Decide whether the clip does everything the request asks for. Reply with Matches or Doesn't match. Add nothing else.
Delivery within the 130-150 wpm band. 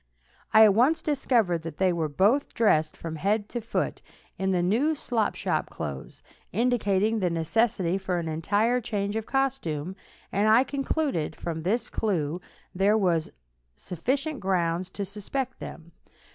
Matches